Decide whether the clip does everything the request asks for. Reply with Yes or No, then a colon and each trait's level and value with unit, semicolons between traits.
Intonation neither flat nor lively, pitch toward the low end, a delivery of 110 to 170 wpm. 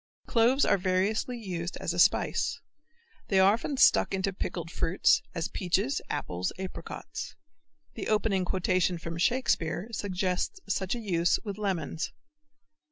No: average, 3.4 semitones; high, 190 Hz; slow, 135 wpm